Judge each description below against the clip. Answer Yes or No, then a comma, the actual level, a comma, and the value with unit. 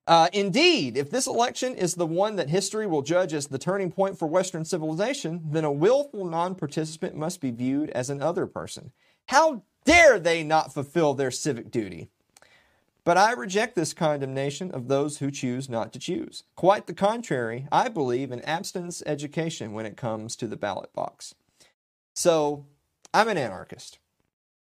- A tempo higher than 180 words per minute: No, average, 170 wpm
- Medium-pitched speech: Yes, medium, 160 Hz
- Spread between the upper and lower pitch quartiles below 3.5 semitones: No, average, 5.1 semitones